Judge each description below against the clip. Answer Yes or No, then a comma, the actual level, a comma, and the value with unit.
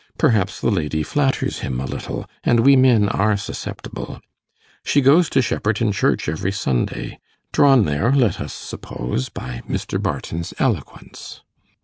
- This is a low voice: Yes, low, 105 Hz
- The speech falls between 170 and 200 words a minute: No, average, 140 wpm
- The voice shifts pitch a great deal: Yes, wide, 8.9 semitones